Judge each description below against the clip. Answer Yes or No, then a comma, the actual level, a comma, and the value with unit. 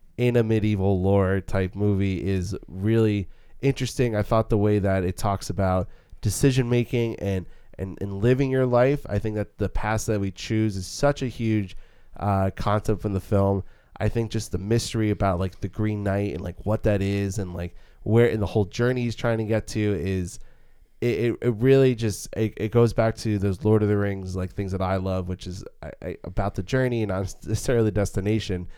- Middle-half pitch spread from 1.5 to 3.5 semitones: Yes, average, 2.7 semitones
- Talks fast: Yes, fast, 215 wpm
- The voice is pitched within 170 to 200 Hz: No, low, 105 Hz